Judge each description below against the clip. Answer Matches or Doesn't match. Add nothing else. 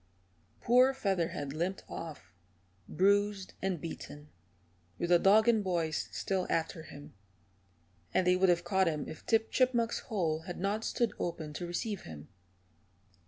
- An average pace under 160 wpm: Matches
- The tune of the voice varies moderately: Matches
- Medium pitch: Matches